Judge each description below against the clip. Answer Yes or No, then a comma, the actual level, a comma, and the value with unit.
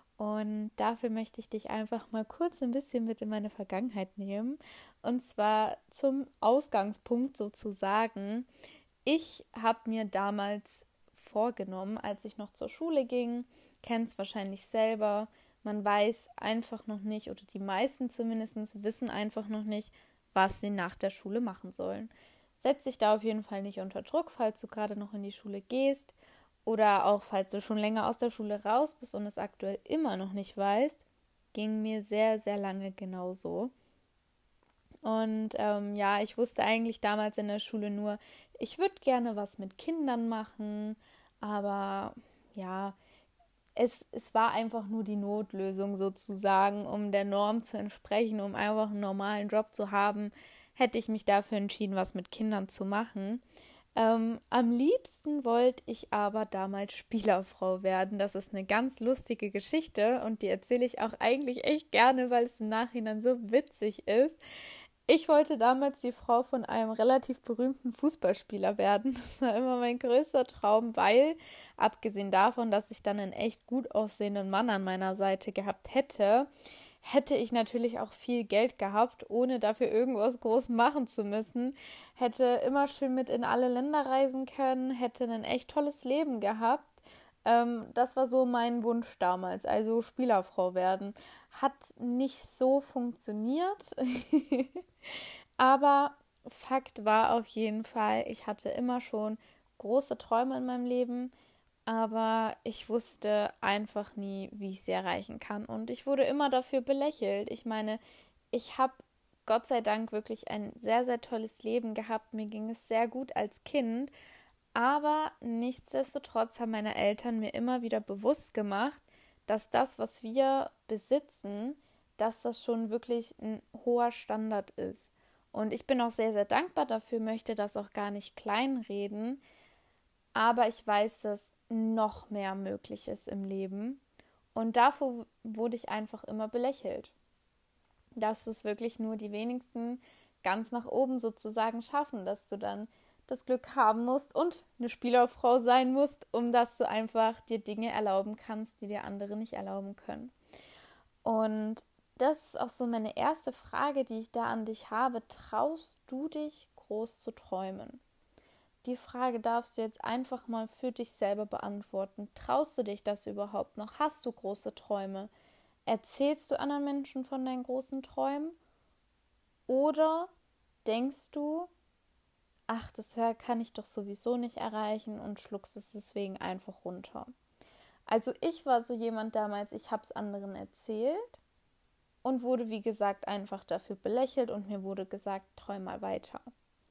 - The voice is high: Yes, high, 225 Hz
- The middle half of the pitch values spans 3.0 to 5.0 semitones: Yes, average, 3.3 semitones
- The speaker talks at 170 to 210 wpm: No, average, 155 wpm